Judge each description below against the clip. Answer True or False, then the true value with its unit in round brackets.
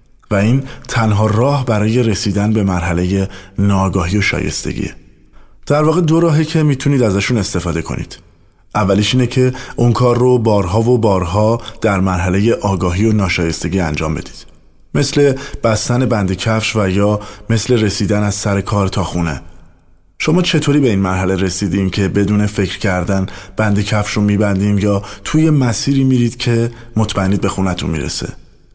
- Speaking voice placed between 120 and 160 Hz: False (105 Hz)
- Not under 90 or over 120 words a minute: False (150 wpm)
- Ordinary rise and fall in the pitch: True (3.8 semitones)